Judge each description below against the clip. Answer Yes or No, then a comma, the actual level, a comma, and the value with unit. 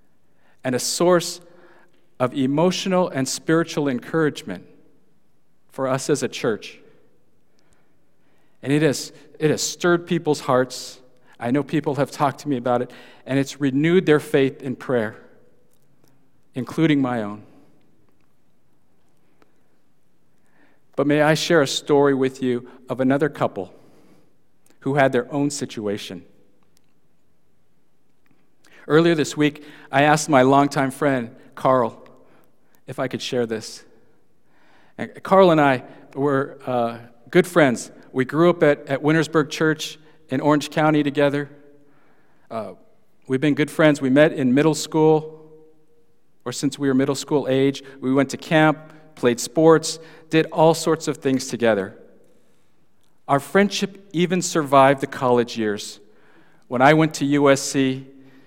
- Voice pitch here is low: No, medium, 145 Hz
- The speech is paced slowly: Yes, slow, 130 wpm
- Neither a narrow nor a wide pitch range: Yes, average, 3.0 semitones